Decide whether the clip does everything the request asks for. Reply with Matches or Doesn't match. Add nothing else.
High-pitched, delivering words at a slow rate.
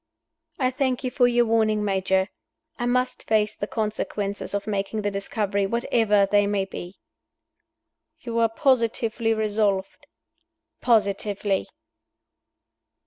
Matches